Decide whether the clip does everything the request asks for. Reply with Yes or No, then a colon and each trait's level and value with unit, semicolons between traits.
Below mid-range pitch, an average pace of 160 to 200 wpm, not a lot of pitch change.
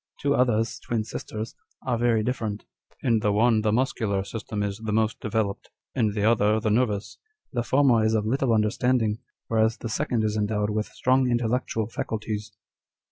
Yes: low, 110 Hz; average, 175 wpm; narrow, 2.1 semitones